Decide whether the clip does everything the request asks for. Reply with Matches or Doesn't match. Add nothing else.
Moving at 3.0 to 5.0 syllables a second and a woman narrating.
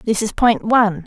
Matches